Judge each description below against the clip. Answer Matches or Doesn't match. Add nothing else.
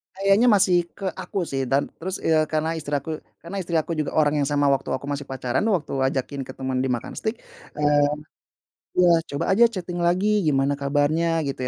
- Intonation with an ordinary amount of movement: Matches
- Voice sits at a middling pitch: Matches